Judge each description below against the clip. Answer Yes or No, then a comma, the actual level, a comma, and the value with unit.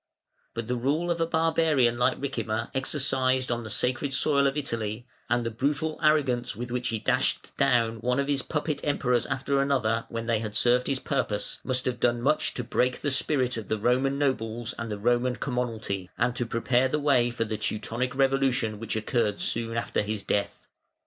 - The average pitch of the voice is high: No, low, 125 Hz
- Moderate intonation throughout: Yes, average, 3.1 semitones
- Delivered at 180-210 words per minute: Yes, average, 195 wpm